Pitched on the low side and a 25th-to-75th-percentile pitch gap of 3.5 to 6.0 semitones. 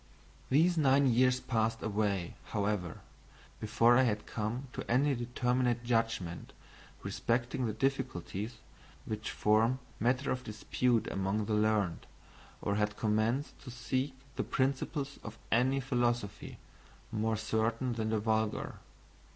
No: low, 115 Hz; average, 3.0 semitones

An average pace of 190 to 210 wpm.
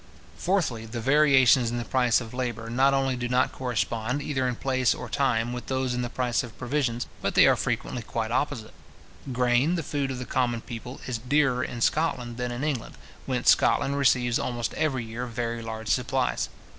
Yes: average, 195 wpm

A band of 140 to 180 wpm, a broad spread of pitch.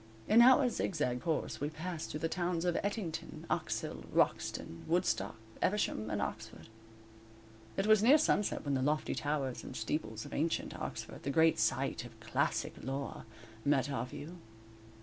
Yes: average, 155 wpm; wide, 6.0 semitones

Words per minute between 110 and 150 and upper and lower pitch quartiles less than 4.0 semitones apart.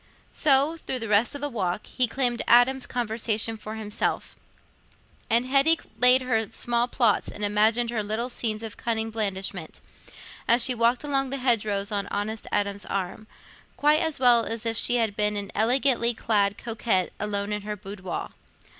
No: average, 170 wpm; average, 3.1 semitones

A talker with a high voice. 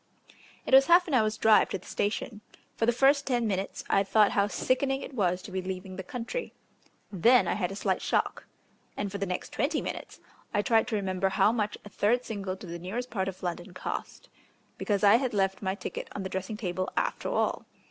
Yes: high, 205 Hz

